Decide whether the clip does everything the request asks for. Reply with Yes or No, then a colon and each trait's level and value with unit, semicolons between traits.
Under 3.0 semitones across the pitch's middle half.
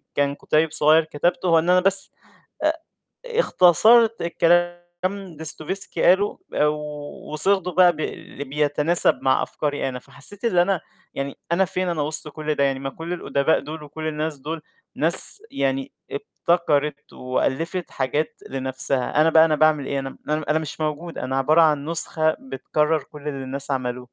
No: average, 3.6 semitones